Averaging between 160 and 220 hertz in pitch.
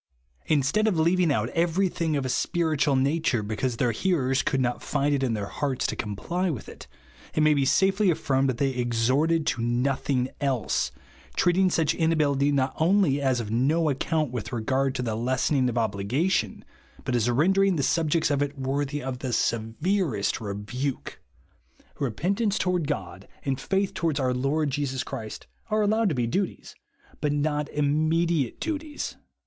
No: medium, 140 Hz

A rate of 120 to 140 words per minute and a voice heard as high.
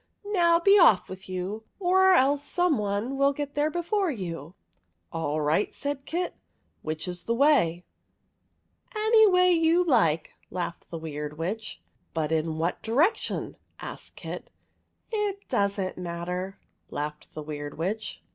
No: average, 165 wpm; high, 205 Hz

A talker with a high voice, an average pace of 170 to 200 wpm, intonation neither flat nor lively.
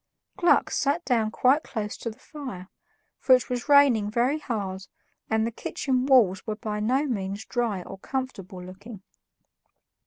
No: high, 230 Hz; average, 155 wpm; average, 4.4 semitones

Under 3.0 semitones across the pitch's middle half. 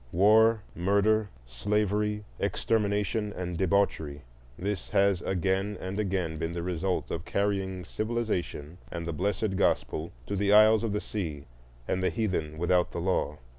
No: average, 3.4 semitones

